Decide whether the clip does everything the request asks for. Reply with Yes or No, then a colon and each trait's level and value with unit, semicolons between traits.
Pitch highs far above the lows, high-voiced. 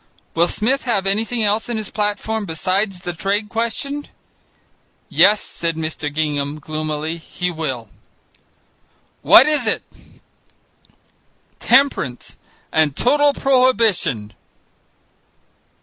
Yes: wide, 6.3 semitones; high, 195 Hz